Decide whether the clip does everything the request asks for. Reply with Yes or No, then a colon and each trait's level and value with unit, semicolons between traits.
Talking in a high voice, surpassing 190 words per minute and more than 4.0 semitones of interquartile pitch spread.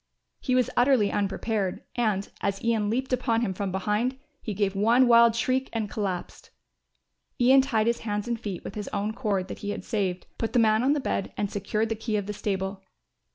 No: high, 215 Hz; fast, 205 wpm; average, 2.9 semitones